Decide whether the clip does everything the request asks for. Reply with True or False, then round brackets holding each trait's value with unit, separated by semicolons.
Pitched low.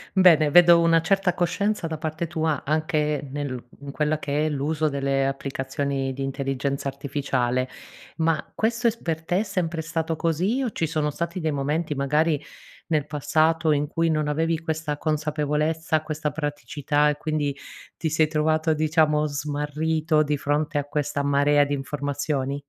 False (150 Hz)